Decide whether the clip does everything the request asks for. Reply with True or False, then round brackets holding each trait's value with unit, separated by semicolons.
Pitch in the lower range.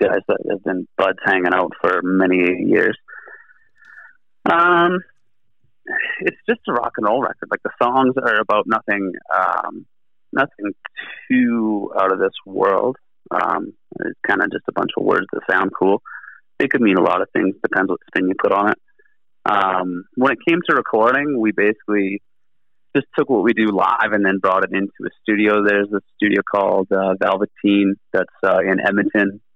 True (105 Hz)